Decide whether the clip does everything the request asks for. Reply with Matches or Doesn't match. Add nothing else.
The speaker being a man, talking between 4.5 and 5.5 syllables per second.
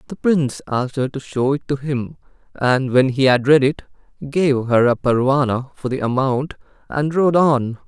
Matches